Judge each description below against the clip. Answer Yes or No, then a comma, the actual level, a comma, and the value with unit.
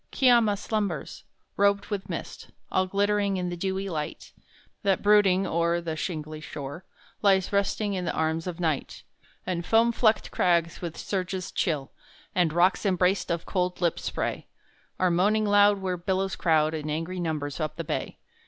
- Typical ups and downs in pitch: Yes, average, 3.2 semitones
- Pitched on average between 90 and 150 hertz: No, medium, 180 Hz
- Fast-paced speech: No, average, 160 wpm